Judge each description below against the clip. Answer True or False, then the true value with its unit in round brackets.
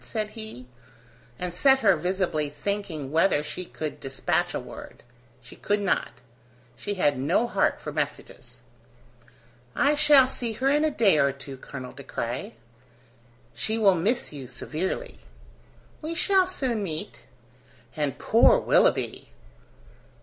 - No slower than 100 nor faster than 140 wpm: True (135 wpm)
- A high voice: True (195 Hz)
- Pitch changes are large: True (8.6 semitones)